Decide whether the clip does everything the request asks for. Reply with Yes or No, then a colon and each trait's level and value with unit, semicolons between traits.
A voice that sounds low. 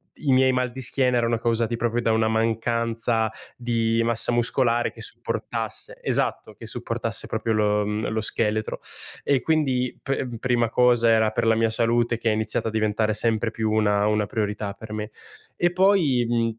Yes: low, 115 Hz